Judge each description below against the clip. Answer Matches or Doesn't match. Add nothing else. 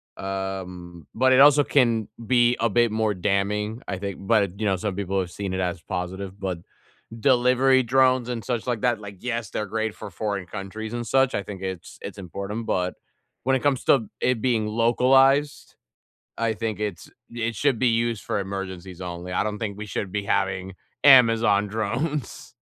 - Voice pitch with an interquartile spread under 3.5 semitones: Doesn't match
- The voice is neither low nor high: Doesn't match